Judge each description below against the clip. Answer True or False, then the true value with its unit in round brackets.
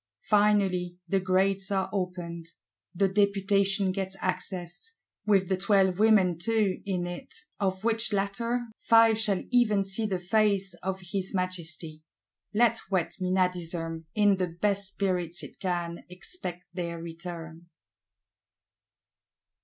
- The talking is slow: True (120 wpm)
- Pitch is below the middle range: False (190 Hz)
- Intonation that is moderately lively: False (2.3 semitones)